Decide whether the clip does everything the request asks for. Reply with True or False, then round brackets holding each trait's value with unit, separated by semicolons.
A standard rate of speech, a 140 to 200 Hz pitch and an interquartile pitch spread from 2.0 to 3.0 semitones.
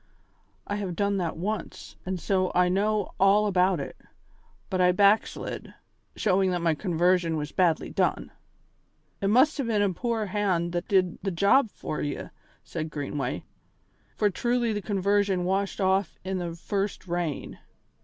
True (155 wpm; 190 Hz; 2.7 semitones)